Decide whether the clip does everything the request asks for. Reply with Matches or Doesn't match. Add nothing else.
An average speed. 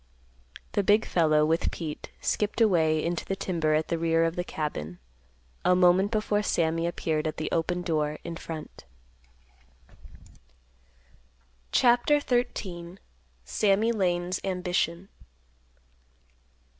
Doesn't match